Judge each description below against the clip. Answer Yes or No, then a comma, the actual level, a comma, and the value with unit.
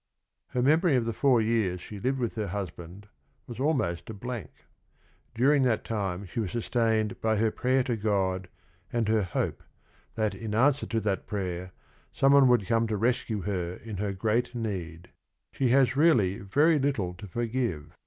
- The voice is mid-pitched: No, low, 110 Hz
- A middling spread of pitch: Yes, average, 4.2 semitones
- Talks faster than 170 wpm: Yes, average, 180 wpm